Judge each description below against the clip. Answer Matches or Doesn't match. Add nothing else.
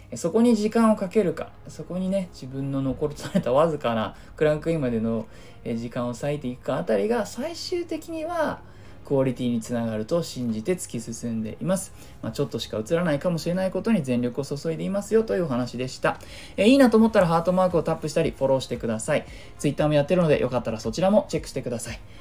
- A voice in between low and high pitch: Matches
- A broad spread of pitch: Matches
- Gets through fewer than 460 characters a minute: Doesn't match